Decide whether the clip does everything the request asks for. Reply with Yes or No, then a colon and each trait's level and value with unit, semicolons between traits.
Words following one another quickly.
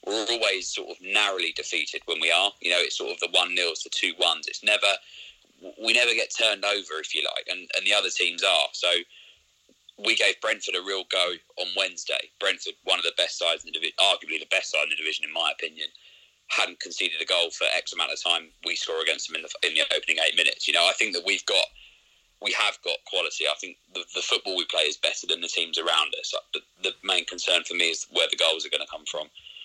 Yes: fast, 250 wpm